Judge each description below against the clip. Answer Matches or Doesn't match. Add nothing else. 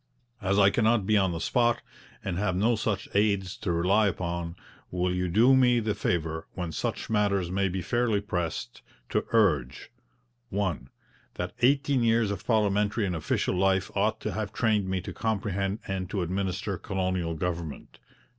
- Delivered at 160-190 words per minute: Matches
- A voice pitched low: Matches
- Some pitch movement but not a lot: Matches